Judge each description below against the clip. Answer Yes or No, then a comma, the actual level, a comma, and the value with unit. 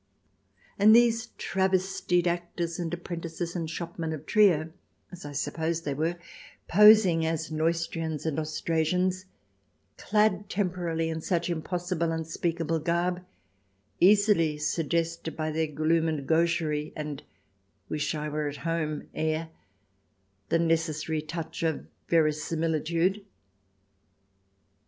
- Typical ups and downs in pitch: No, narrow, 1.9 semitones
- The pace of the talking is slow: Yes, slow, 115 wpm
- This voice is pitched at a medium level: Yes, medium, 165 Hz